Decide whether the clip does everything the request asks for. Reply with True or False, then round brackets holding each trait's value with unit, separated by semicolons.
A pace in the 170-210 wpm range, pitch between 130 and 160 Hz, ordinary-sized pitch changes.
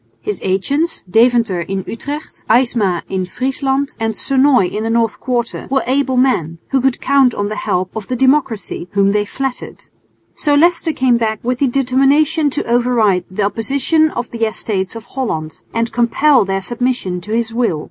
False (175 wpm; 240 Hz; 4.5 semitones)